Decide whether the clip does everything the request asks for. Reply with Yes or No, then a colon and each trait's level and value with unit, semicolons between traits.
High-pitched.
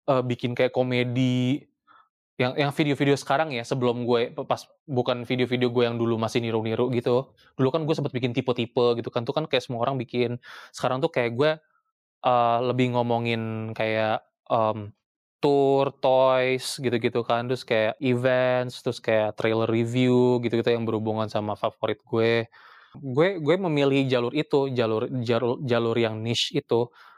No: low, 125 Hz